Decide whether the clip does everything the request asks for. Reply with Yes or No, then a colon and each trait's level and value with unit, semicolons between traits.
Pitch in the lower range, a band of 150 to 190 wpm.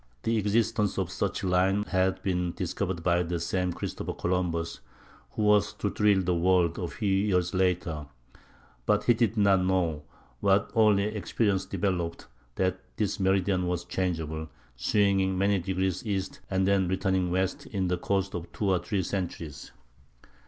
Yes: very low, 95 Hz; average, 160 wpm